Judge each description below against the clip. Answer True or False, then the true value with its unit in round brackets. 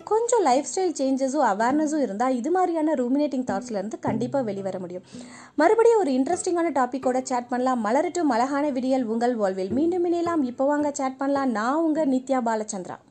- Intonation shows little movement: False (4.0 semitones)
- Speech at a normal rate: False (150 wpm)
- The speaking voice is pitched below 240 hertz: False (265 Hz)